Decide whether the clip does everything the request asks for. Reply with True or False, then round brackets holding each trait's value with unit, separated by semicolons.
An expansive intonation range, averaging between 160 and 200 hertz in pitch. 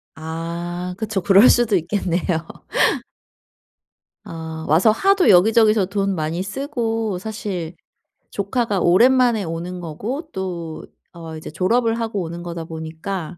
False (4.8 semitones; 185 Hz)